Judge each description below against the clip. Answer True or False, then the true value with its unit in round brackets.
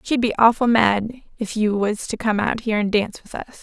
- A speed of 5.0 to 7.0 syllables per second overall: True (5.5 syllables/s)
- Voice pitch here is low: False (220 Hz)